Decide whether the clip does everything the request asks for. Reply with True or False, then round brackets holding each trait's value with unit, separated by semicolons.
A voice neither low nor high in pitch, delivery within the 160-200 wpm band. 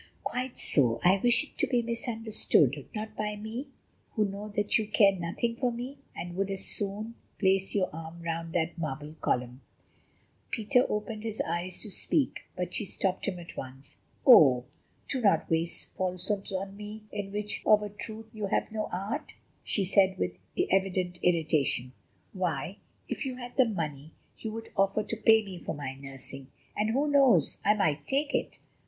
False (195 Hz; 175 wpm)